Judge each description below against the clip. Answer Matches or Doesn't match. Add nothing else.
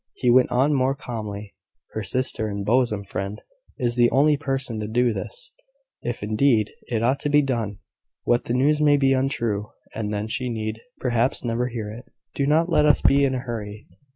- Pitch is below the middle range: Matches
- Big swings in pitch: Doesn't match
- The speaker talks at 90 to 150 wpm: Doesn't match